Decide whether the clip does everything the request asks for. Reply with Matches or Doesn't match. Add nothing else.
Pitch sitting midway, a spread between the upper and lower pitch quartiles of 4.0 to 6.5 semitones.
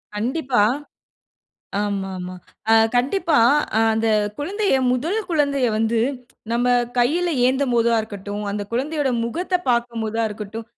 Doesn't match